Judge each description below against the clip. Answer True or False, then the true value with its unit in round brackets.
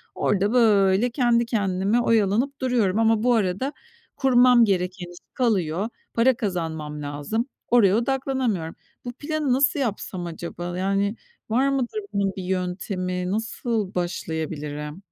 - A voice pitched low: False (205 Hz)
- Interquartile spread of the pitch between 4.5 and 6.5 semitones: True (5.1 semitones)